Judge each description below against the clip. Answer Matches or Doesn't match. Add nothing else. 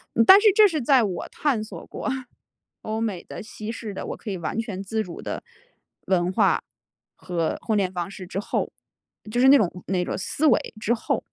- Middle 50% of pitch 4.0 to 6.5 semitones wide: Matches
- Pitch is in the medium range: Doesn't match